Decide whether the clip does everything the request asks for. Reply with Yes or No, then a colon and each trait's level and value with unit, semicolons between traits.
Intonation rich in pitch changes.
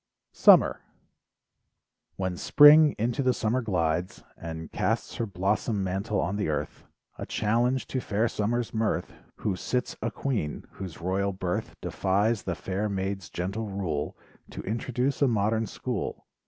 No: average, 3.8 semitones